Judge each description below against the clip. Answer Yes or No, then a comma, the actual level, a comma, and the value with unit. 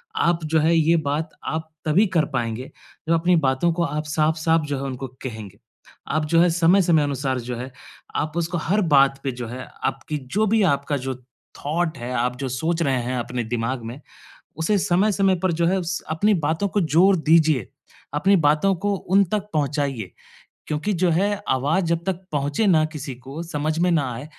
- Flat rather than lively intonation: No, average, 4.2 semitones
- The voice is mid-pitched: Yes, medium, 155 Hz